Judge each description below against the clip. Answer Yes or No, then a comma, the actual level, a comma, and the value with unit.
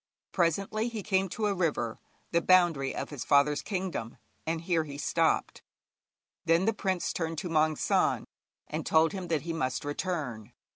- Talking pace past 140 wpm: Yes, average, 165 wpm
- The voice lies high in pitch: No, medium, 165 Hz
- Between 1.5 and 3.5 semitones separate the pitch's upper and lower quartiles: No, average, 4.1 semitones